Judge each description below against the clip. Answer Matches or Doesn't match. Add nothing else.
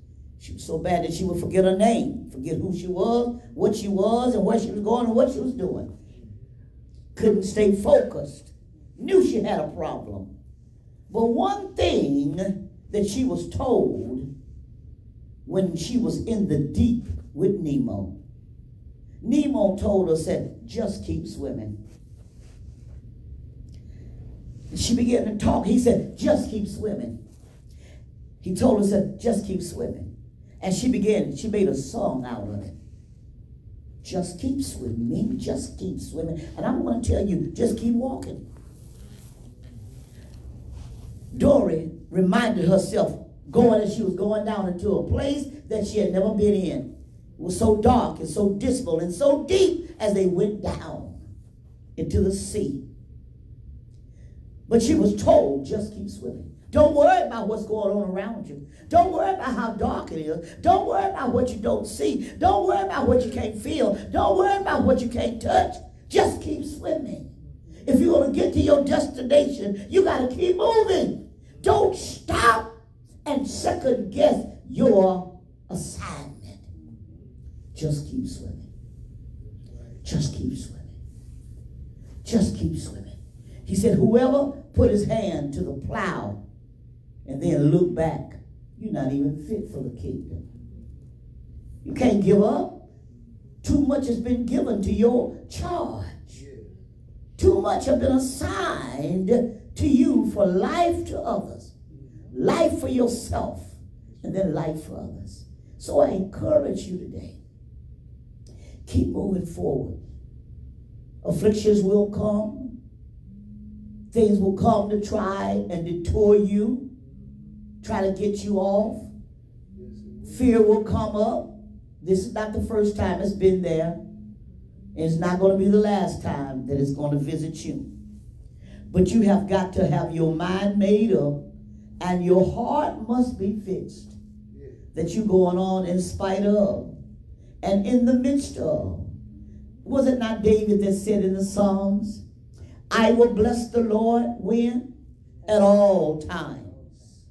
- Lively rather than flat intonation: Matches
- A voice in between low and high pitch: Doesn't match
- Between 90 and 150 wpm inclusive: Matches